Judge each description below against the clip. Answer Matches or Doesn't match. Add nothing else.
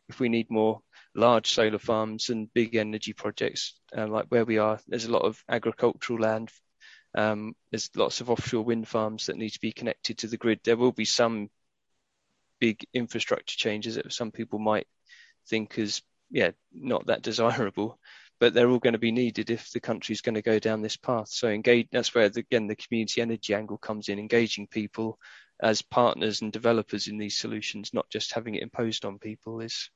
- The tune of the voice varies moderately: Doesn't match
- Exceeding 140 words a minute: Matches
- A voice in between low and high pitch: Doesn't match